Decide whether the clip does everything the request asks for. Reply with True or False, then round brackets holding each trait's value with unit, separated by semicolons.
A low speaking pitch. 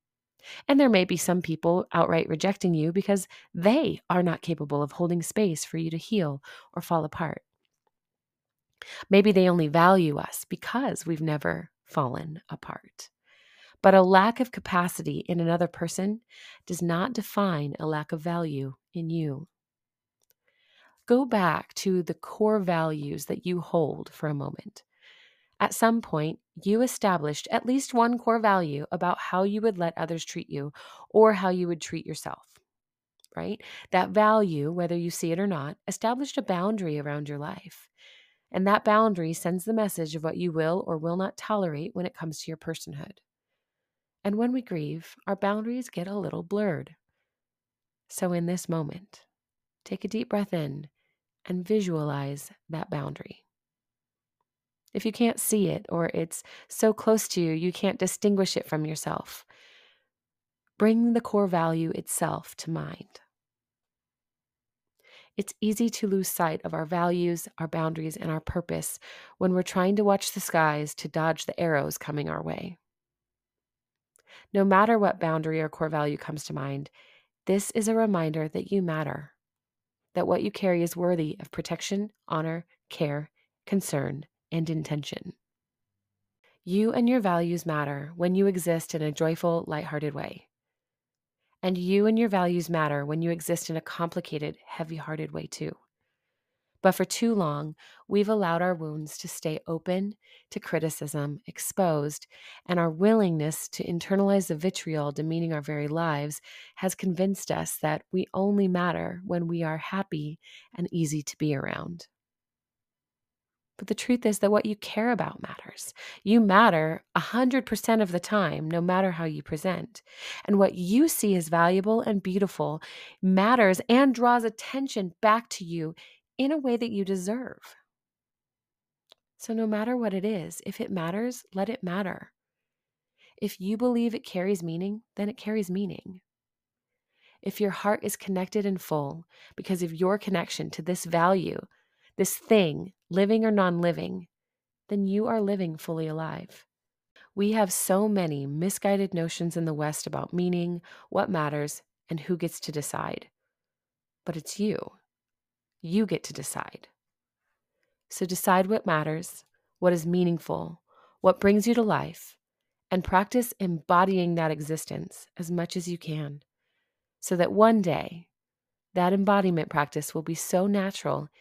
False (180 Hz)